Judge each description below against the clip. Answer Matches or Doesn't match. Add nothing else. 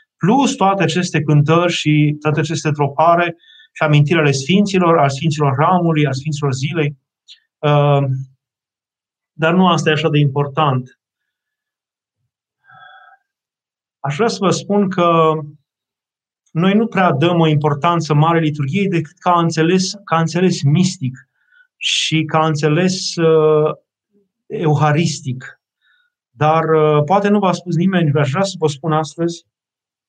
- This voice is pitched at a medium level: Matches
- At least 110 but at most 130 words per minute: Matches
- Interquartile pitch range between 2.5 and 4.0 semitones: Matches